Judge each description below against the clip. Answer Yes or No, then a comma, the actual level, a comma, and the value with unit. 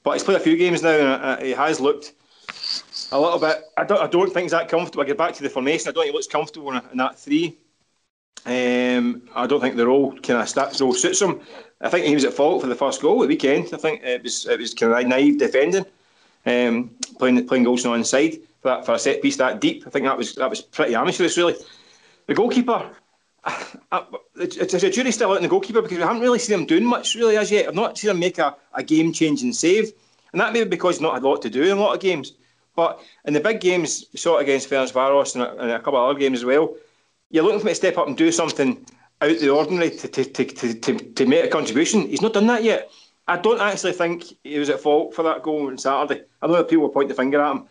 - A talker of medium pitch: Yes, medium, 165 Hz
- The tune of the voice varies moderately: No, wide, 7.3 semitones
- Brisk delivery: Yes, fast, 265 wpm